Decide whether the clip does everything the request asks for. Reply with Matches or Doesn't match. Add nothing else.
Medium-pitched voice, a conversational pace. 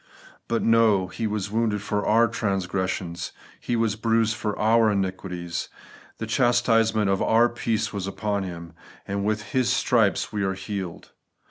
Doesn't match